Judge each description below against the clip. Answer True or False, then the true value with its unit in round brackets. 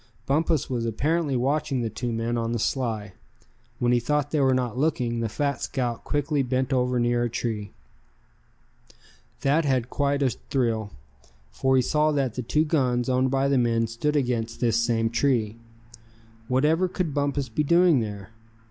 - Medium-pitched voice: False (125 Hz)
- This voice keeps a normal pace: True (170 wpm)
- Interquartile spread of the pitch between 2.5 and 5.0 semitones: True (3.5 semitones)